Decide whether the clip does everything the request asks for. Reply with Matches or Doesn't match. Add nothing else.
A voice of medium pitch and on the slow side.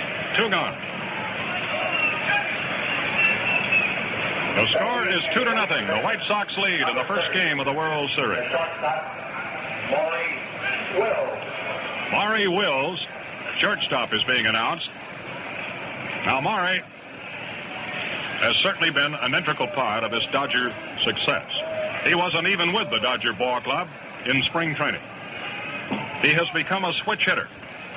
Matches